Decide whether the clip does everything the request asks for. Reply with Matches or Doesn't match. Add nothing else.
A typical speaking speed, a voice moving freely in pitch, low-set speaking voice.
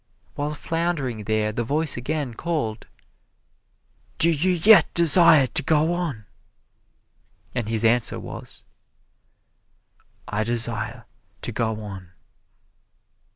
Doesn't match